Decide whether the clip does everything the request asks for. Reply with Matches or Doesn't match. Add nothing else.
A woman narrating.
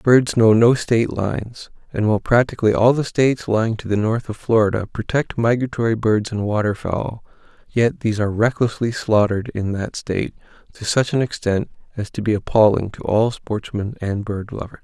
Doesn't match